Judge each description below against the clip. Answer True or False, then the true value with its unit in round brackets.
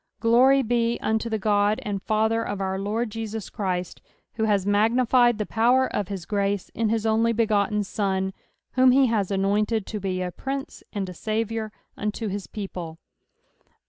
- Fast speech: False (170 wpm)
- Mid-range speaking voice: False (215 Hz)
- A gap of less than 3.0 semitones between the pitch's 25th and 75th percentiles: True (2.4 semitones)